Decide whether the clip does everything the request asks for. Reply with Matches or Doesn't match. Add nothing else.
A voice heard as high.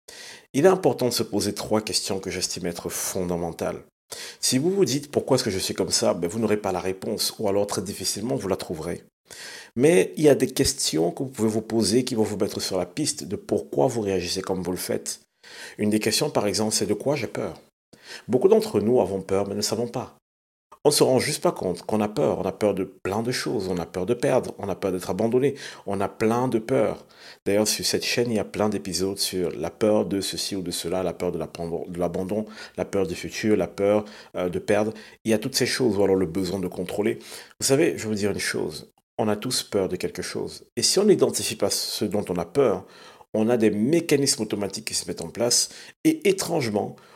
Doesn't match